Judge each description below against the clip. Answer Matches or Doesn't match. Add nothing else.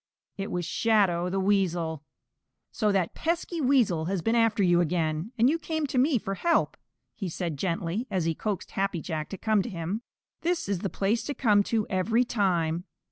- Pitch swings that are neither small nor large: Matches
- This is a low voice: Doesn't match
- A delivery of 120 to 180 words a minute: Doesn't match